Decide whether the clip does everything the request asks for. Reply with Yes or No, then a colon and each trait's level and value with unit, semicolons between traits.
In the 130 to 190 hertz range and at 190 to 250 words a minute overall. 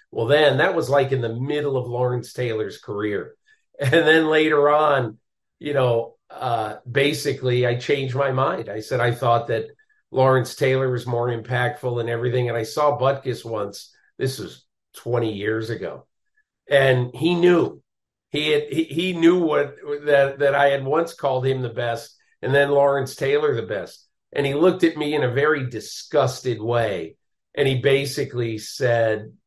No: low, 135 Hz; average, 170 wpm